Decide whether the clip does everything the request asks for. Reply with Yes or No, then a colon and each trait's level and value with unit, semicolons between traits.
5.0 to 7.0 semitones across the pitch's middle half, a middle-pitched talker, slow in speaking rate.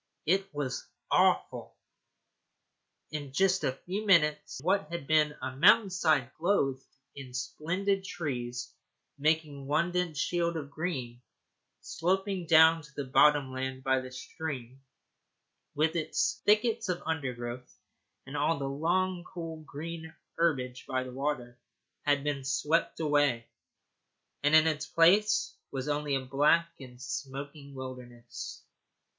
No: average, 4.2 semitones; medium, 150 Hz; slow, 130 wpm